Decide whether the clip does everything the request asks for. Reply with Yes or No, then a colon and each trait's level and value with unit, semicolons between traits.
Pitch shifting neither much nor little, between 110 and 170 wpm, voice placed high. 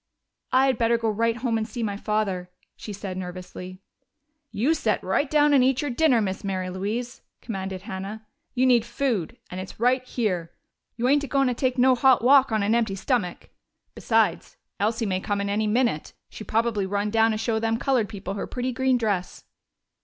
No: average, 4.0 semitones; average, 200 wpm; high, 225 Hz